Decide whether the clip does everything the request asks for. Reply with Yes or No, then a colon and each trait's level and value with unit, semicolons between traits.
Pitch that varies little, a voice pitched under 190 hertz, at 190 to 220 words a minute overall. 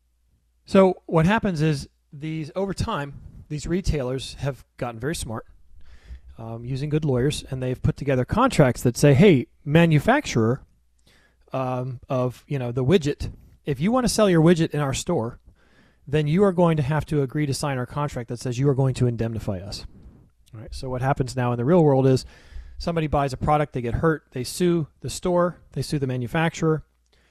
No: average, 4.6 semitones; medium, 140 Hz; average, 195 wpm